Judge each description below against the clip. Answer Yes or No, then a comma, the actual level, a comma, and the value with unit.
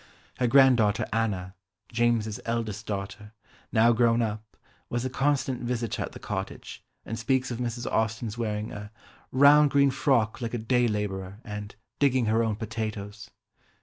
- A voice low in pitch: Yes, low, 115 Hz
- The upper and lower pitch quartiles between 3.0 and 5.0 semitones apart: No, narrow, 2.6 semitones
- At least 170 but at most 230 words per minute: No, average, 150 wpm